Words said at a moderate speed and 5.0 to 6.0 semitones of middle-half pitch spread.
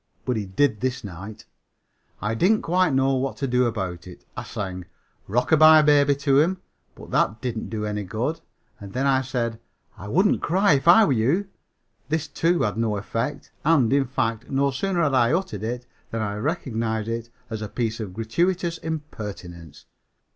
Yes: average, 180 wpm; wide, 5.6 semitones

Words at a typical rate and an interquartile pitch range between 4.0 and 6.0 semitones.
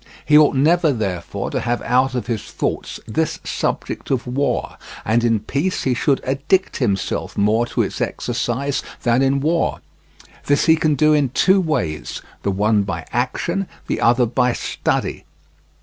Yes: average, 165 wpm; average, 4.3 semitones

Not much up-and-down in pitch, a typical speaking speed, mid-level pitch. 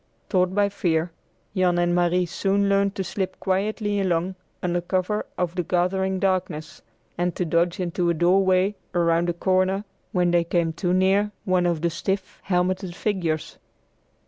Yes: narrow, 1.7 semitones; average, 165 wpm; medium, 180 Hz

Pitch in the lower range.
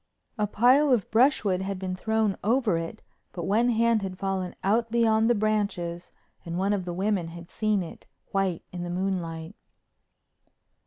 No: high, 195 Hz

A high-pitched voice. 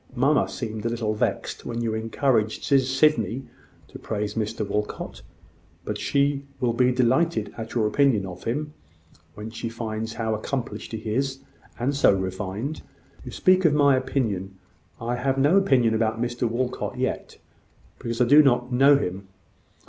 No: low, 120 Hz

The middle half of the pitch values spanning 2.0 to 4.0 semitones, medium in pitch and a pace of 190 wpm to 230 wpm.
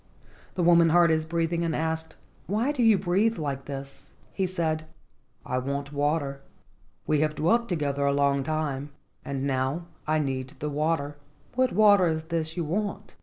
No: average, 3.6 semitones; medium, 160 Hz; average, 170 wpm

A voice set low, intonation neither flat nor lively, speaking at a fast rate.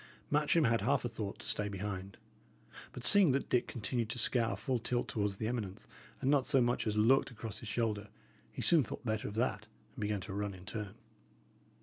Yes: low, 115 Hz; average, 3.2 semitones; fast, 210 wpm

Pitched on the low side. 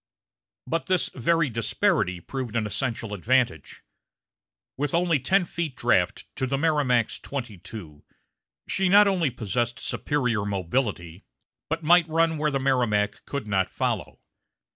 Yes: low, 130 Hz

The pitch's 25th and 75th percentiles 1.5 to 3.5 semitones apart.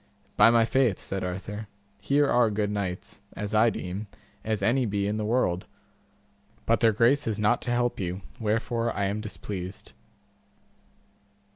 Yes: average, 2.7 semitones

